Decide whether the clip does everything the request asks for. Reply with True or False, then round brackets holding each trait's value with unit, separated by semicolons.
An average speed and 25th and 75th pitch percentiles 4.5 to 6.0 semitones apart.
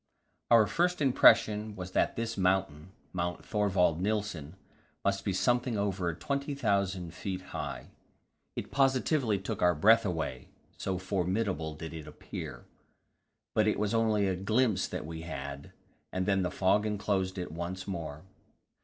False (145 wpm; 3.6 semitones)